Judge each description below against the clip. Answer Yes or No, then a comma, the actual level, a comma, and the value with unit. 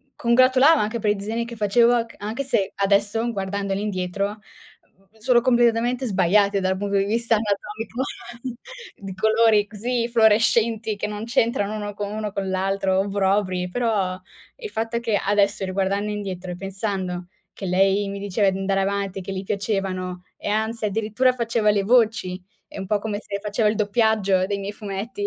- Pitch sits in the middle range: No, high, 205 Hz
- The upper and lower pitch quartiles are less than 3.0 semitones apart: Yes, narrow, 2.6 semitones